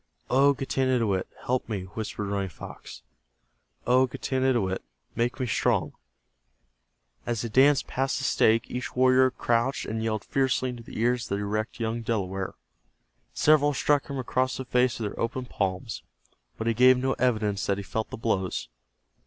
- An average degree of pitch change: Yes, average, 3.3 semitones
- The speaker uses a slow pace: No, average, 160 wpm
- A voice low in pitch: Yes, low, 120 Hz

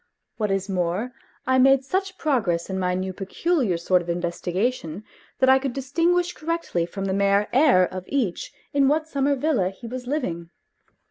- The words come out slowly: No, average, 175 wpm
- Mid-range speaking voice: No, high, 230 Hz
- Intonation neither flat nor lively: No, wide, 7.2 semitones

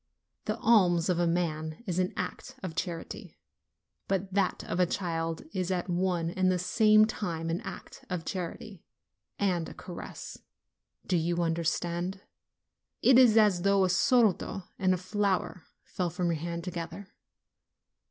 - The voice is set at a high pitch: No, medium, 180 Hz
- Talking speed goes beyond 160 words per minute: No, average, 155 wpm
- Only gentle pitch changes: Yes, narrow, 2.3 semitones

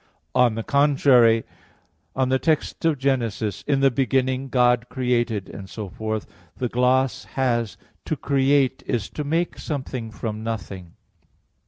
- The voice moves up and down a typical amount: Yes, average, 3.1 semitones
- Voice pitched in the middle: No, low, 125 Hz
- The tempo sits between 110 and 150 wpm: Yes, slow, 135 wpm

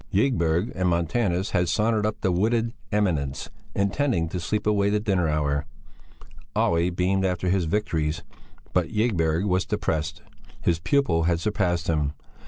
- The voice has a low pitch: Yes, very low, 90 Hz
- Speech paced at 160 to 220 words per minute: No, average, 145 wpm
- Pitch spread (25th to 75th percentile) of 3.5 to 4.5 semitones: Yes, average, 4.1 semitones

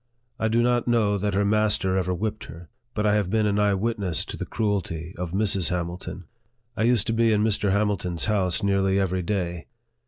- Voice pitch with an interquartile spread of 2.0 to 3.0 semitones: Yes, average, 2.7 semitones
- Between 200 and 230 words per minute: Yes, fast, 205 wpm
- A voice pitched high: No, low, 100 Hz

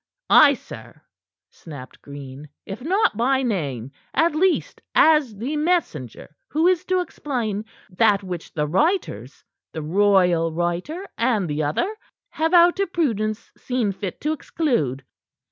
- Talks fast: No, slow, 135 wpm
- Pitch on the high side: Yes, high, 215 Hz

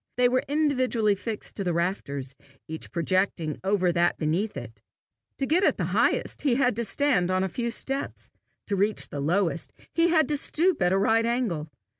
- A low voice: No, high, 205 Hz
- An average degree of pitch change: No, wide, 6.7 semitones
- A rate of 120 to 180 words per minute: No, average, 190 wpm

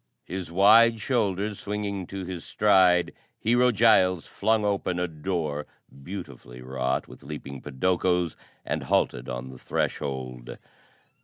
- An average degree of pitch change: No, wide, 6.5 semitones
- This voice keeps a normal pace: No, slow, 125 wpm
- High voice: No, very low, 90 Hz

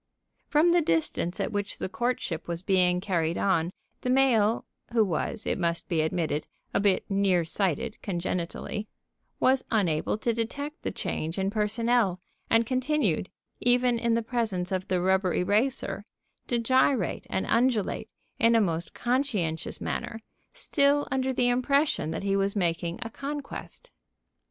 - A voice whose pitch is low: No, high, 210 Hz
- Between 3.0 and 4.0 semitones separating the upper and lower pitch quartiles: No, wide, 5.5 semitones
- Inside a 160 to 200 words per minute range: No, average, 150 wpm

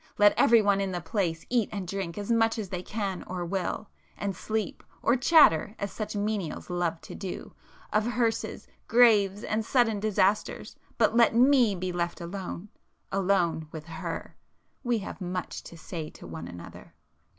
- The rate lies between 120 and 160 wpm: Yes, average, 150 wpm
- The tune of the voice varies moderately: Yes, average, 3.8 semitones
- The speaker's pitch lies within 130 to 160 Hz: No, high, 200 Hz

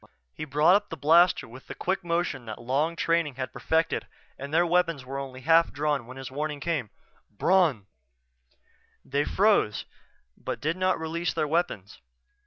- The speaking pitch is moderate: Yes, medium, 155 Hz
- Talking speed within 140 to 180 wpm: Yes, average, 165 wpm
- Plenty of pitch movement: No, average, 4.1 semitones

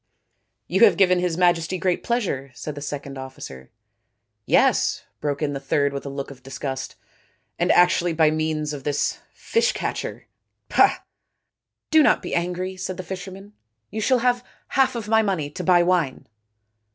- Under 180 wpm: No, average, 185 wpm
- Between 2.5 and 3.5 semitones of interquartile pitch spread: No, average, 5.0 semitones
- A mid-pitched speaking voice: Yes, medium, 170 Hz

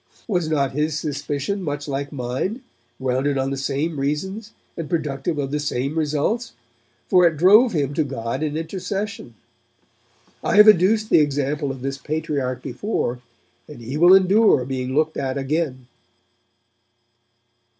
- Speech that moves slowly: No, average, 145 wpm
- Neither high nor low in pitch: Yes, medium, 150 Hz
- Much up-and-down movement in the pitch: No, average, 4.4 semitones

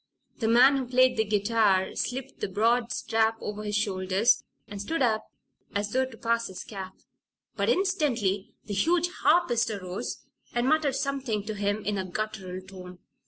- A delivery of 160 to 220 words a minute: Yes, average, 165 wpm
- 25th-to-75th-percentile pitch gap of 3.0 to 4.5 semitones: Yes, average, 4.0 semitones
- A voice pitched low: No, high, 220 Hz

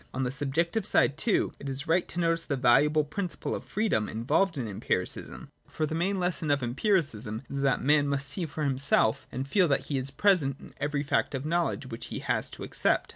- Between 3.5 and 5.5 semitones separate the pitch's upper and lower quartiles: Yes, average, 3.9 semitones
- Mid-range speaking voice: Yes, medium, 145 Hz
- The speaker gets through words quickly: Yes, fast, 215 wpm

